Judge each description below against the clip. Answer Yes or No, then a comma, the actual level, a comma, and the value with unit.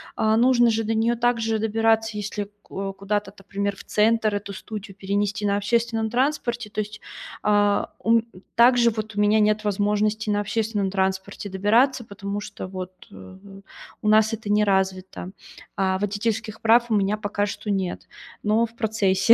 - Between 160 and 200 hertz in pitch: No, high, 210 Hz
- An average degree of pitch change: No, narrow, 1.9 semitones